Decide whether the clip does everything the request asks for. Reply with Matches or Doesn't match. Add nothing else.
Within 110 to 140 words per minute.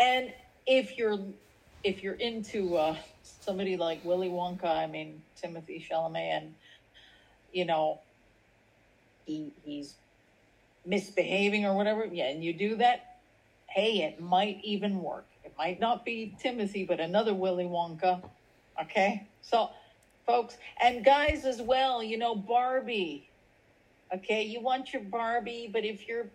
Matches